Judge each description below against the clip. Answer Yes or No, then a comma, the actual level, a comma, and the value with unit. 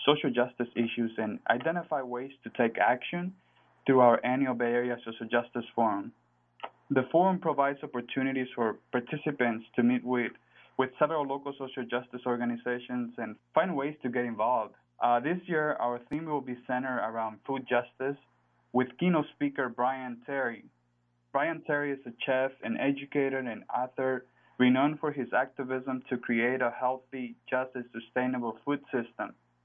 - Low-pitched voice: Yes, low, 125 Hz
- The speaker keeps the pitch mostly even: Yes, narrow, 2.3 semitones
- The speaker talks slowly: No, average, 155 wpm